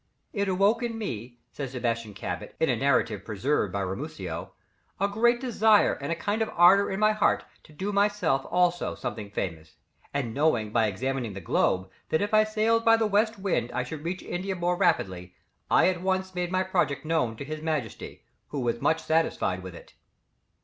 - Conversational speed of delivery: Yes, average, 190 wpm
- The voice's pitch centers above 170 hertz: No, medium, 165 Hz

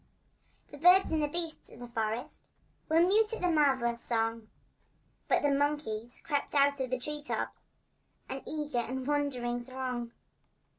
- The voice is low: No, very high, 275 Hz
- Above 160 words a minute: No, average, 155 wpm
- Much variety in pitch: No, average, 3.8 semitones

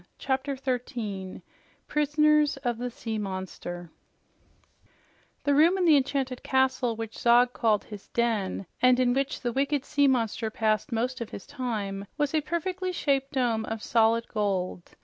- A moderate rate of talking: Yes, average, 150 wpm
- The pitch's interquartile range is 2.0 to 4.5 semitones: Yes, average, 4.1 semitones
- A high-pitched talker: Yes, high, 245 Hz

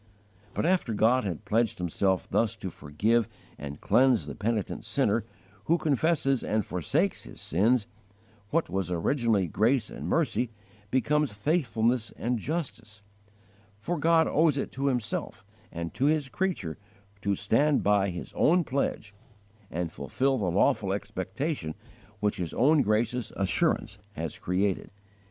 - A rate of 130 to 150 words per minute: Yes, average, 140 wpm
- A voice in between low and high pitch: No, low, 115 Hz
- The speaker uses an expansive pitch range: Yes, wide, 5.9 semitones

